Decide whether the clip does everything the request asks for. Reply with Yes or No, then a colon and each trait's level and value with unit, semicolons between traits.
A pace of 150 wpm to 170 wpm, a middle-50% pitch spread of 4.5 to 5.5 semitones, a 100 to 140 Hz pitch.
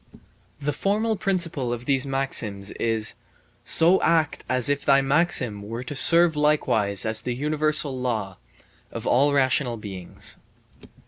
No: slow, 135 wpm; average, 4.9 semitones; low, 135 Hz